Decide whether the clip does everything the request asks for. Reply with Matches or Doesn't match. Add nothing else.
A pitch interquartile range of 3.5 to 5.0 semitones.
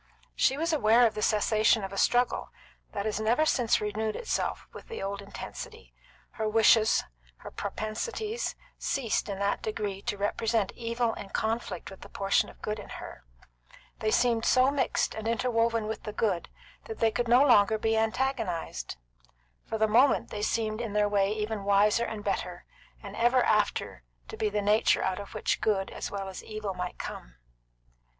Doesn't match